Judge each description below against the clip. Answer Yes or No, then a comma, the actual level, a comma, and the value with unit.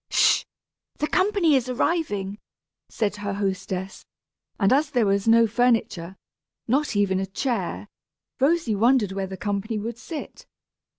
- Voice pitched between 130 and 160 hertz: No, high, 215 Hz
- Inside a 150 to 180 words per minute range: No, average, 140 wpm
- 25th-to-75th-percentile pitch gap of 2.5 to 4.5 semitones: No, average, 4.9 semitones